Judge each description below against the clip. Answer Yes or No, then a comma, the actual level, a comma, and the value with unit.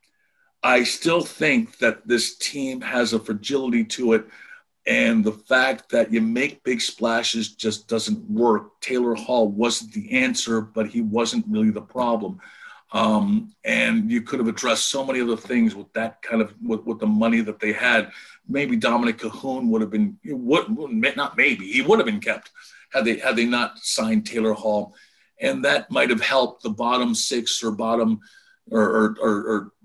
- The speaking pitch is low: Yes, low, 120 Hz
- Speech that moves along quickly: No, average, 180 wpm